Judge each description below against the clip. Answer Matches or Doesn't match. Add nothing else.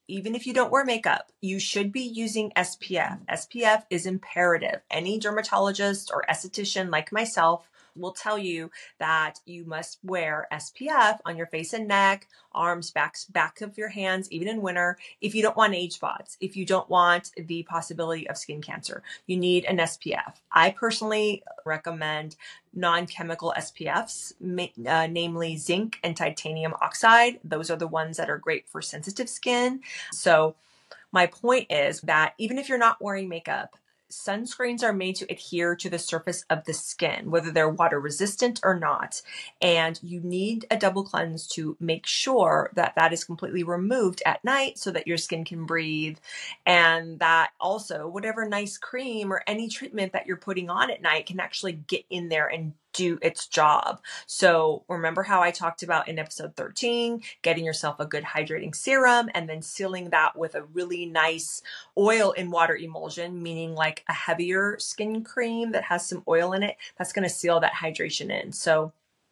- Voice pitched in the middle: Matches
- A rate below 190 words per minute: Matches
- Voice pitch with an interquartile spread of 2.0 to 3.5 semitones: Doesn't match